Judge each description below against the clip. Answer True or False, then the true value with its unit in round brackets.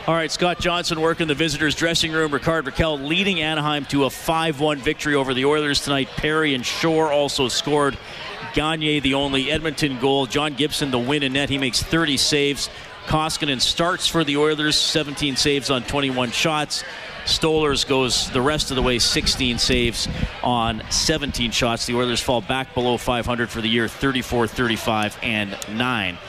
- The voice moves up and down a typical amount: True (3.9 semitones)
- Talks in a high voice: False (140 Hz)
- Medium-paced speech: True (175 wpm)